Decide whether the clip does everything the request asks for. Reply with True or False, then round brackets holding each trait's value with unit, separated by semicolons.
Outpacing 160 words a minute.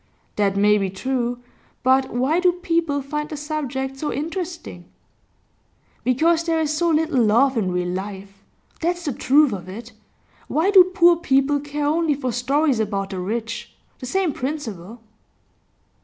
False (155 wpm)